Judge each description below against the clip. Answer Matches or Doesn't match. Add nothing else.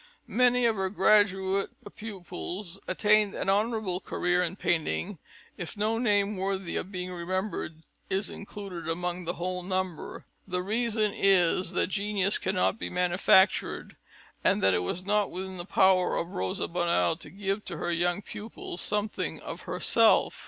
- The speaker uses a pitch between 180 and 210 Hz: Matches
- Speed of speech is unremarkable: Matches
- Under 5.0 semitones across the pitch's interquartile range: Matches